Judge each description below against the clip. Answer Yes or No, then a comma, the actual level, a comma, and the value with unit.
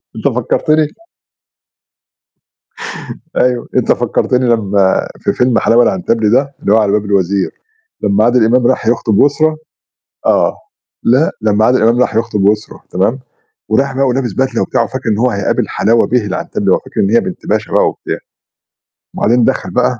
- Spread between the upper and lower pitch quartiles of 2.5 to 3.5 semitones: Yes, average, 3.2 semitones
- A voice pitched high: No, low, 115 Hz